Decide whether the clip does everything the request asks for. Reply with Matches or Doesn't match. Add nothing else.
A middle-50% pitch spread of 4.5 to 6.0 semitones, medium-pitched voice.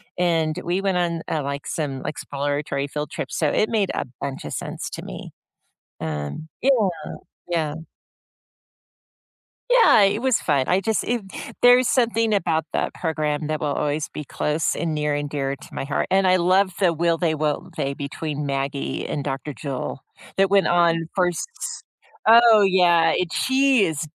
Matches